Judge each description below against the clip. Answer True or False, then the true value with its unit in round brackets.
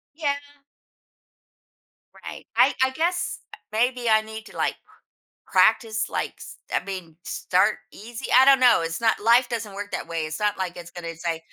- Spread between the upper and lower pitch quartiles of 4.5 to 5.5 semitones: True (5.1 semitones)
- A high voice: True (215 Hz)